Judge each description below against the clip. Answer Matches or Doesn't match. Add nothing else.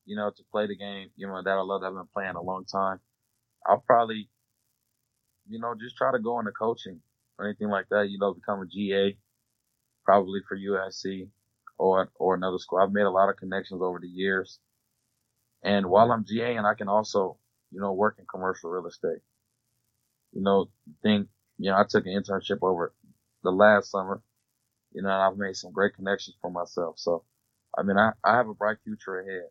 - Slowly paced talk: Doesn't match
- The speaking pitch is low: Matches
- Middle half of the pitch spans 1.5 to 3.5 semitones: Matches